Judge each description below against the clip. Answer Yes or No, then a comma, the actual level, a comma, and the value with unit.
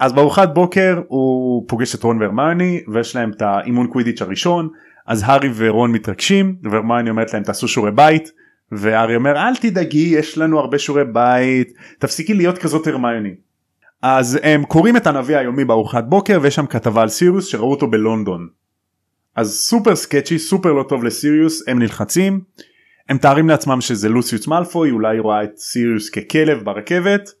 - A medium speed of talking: No, fast, 160 wpm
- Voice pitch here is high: No, low, 135 Hz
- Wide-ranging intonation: Yes, wide, 6.0 semitones